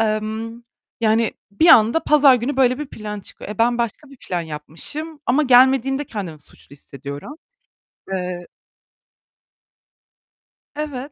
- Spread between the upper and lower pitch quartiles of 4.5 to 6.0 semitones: Yes, average, 5.1 semitones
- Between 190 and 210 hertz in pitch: No, high, 230 Hz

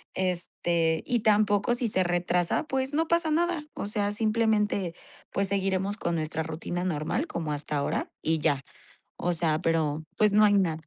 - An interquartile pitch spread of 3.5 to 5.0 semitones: Yes, average, 4.6 semitones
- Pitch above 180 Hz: Yes, high, 190 Hz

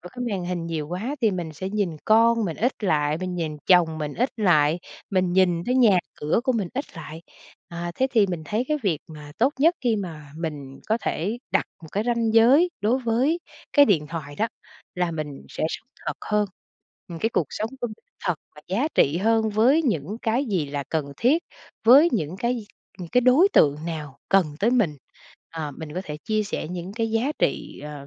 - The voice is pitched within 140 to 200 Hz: Yes, high, 190 Hz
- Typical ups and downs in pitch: No, wide, 6.4 semitones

